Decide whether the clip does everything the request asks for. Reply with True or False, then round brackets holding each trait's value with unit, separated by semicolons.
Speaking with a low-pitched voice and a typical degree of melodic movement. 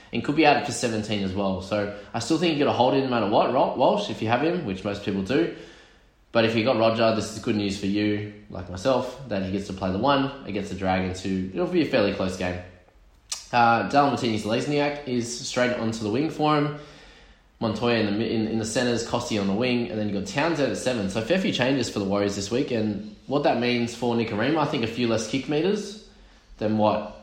True (115 Hz; 3.7 semitones)